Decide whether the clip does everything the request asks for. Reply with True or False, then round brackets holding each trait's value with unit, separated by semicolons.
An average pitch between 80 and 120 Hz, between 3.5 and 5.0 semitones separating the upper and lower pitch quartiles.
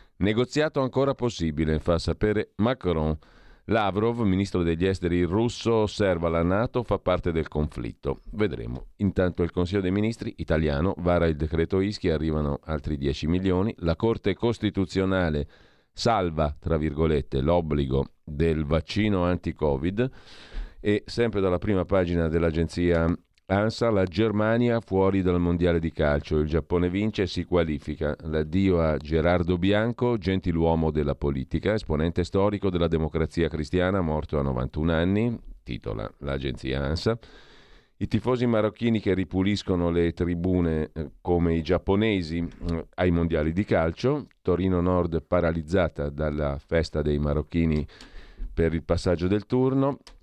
True (90 Hz; 3.9 semitones)